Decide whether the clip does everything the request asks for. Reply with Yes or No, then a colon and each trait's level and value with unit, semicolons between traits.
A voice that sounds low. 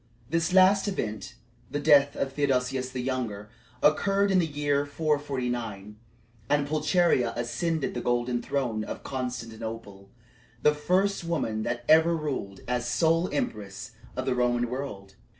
Yes: low, 130 Hz